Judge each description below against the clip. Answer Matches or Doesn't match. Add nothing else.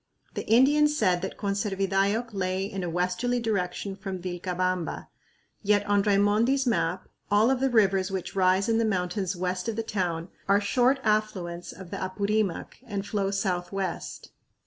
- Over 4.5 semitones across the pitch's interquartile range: Doesn't match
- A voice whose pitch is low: Doesn't match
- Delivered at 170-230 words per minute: Doesn't match